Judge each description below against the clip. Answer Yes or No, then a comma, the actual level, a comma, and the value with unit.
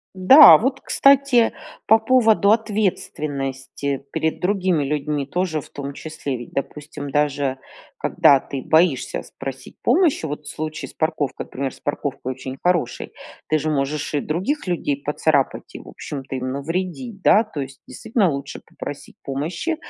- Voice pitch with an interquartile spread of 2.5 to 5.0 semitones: No, wide, 5.5 semitones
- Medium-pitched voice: Yes, medium, 150 Hz